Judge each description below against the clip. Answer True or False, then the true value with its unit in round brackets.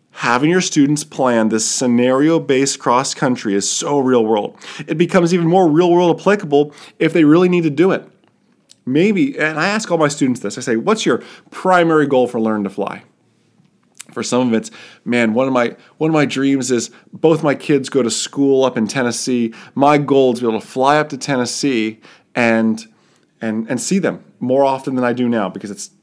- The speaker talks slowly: False (205 wpm)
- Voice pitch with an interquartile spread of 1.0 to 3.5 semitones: False (4.2 semitones)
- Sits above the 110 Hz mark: True (135 Hz)